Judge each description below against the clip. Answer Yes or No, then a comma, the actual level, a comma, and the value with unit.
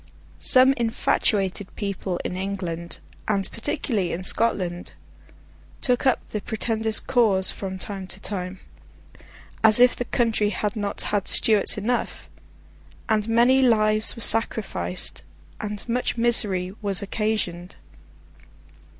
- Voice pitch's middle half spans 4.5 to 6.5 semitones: No, average, 3.3 semitones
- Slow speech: Yes, slow, 110 wpm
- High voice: Yes, high, 210 Hz